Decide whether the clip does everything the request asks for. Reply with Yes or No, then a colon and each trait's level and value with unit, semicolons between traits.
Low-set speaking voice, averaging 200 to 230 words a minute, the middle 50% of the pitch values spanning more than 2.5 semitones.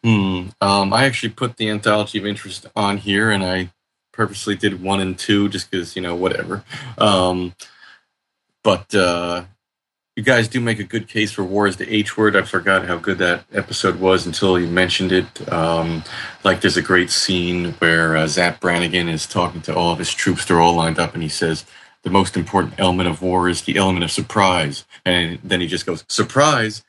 Yes: very low, 95 Hz; fast, 205 wpm; average, 2.9 semitones